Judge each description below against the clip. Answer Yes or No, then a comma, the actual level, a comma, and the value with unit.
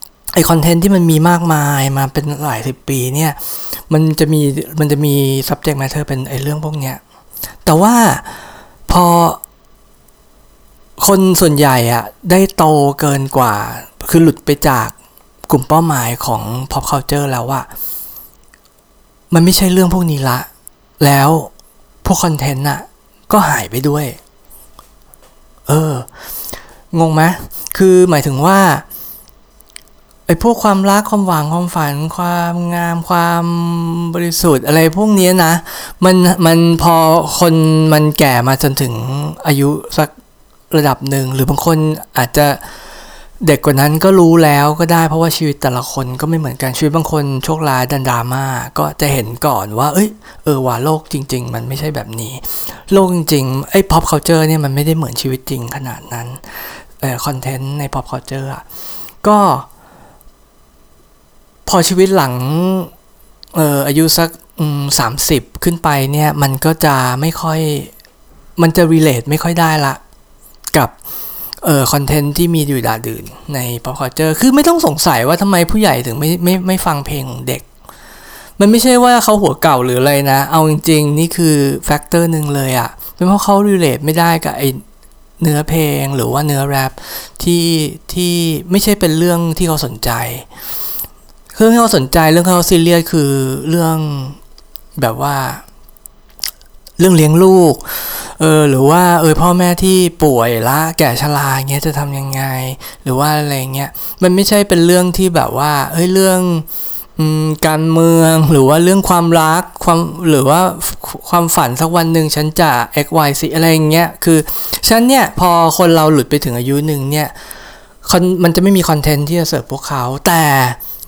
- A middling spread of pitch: Yes, average, 3.6 semitones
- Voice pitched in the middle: Yes, medium, 155 Hz